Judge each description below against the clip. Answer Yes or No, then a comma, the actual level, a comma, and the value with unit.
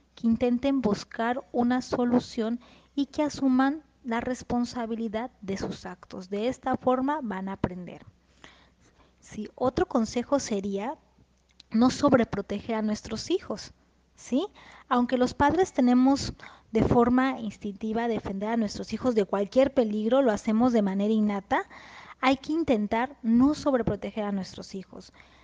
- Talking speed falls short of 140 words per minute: Yes, average, 130 wpm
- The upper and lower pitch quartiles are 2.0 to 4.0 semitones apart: Yes, average, 3.6 semitones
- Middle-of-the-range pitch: No, high, 240 Hz